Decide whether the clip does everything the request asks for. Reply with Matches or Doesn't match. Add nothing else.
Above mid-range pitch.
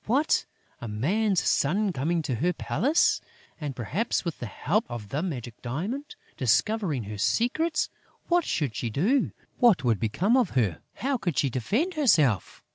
Doesn't match